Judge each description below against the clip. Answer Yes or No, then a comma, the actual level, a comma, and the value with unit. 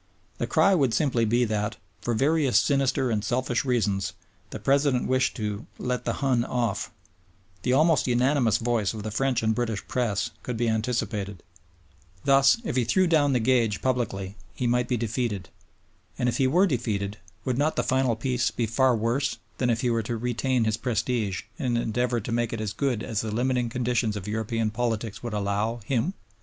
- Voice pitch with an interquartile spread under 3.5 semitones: Yes, average, 2.8 semitones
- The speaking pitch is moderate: No, low, 120 Hz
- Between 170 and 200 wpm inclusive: Yes, average, 190 wpm